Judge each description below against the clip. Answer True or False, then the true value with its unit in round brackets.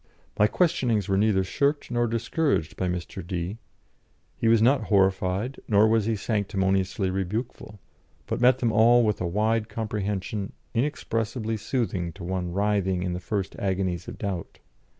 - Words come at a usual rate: True (150 wpm)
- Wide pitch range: False (3.2 semitones)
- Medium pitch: False (105 Hz)